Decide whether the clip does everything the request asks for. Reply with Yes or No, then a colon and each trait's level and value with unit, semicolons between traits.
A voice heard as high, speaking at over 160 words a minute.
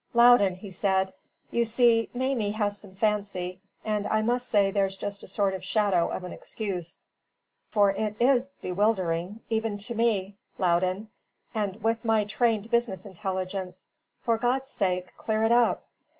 No: high, 205 Hz; average, 155 wpm